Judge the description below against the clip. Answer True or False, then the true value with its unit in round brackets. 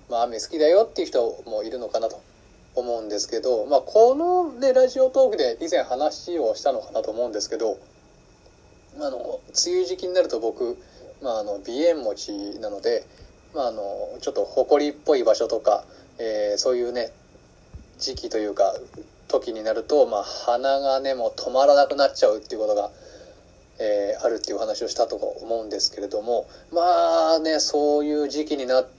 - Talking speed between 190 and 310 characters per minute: True (300 characters per minute)